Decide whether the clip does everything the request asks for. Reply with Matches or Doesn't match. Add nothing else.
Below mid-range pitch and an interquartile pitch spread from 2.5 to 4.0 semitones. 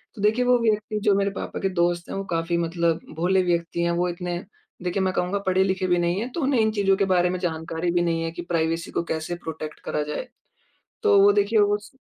Doesn't match